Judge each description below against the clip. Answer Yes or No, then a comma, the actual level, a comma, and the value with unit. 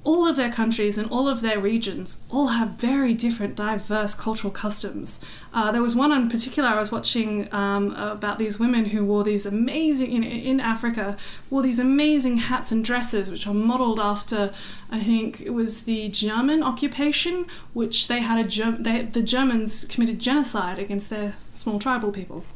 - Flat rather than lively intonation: No, average, 3.1 semitones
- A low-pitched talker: No, high, 225 Hz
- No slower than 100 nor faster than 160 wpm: No, average, 180 wpm